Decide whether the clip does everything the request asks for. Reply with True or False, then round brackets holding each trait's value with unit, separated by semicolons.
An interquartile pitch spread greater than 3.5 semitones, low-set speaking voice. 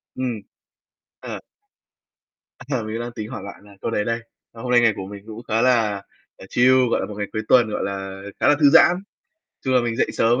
False (3.1 semitones; 115 Hz)